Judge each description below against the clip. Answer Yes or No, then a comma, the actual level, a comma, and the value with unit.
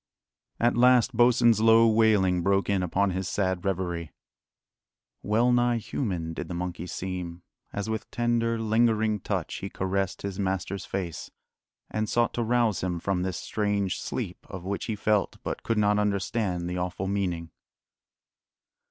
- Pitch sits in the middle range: No, low, 100 Hz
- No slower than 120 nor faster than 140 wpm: No, average, 150 wpm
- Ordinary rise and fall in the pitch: Yes, average, 3.5 semitones